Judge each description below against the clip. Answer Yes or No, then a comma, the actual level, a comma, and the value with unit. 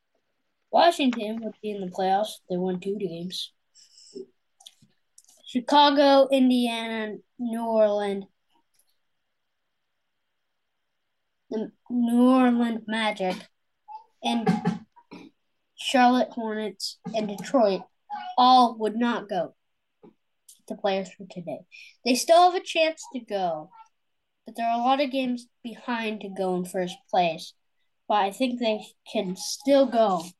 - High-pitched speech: Yes, high, 225 Hz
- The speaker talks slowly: Yes, slow, 115 wpm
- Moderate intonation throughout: Yes, average, 4.3 semitones